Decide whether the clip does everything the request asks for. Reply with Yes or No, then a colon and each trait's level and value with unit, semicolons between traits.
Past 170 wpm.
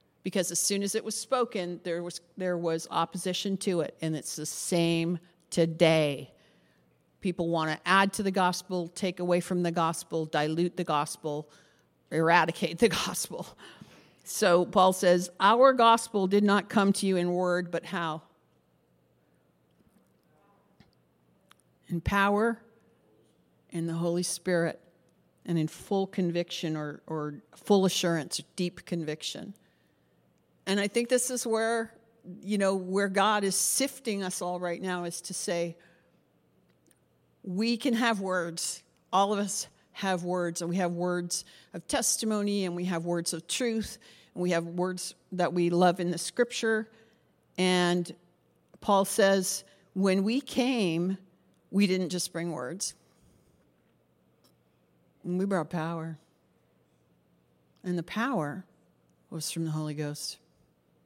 No: slow, 135 wpm